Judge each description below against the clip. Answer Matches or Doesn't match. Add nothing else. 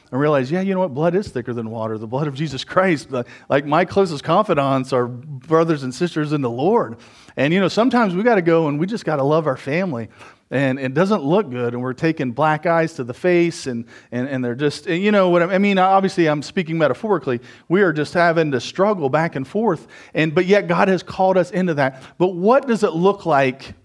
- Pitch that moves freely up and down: Matches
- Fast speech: Matches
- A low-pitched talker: Doesn't match